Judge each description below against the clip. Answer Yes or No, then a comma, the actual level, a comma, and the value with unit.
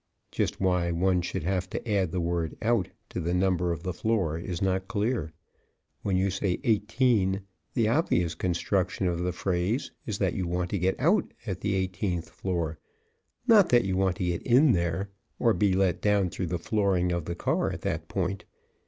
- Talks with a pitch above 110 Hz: No, very low, 95 Hz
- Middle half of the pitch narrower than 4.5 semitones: Yes, average, 2.7 semitones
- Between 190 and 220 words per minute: Yes, average, 195 wpm